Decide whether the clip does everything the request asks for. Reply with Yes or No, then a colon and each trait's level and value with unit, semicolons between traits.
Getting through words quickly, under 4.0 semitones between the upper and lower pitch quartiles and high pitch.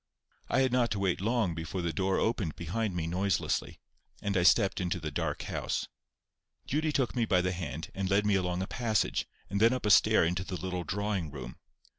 No: fast, 210 wpm; average, 3.5 semitones; very low, 95 Hz